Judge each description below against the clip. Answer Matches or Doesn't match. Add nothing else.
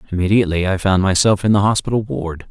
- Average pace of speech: Matches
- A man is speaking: Matches